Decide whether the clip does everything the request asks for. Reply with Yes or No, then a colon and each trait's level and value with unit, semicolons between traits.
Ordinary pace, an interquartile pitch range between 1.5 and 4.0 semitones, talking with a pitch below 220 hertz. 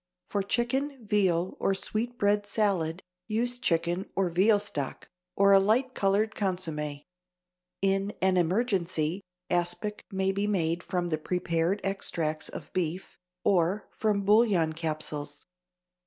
No: slow, 125 wpm; average, 3.6 semitones; high, 190 Hz